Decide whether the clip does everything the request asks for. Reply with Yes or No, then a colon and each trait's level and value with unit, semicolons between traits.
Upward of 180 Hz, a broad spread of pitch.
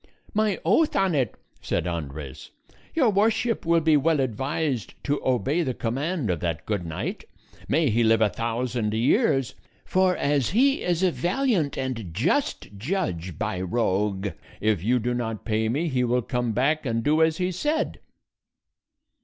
No: low, 130 Hz; wide, 7.5 semitones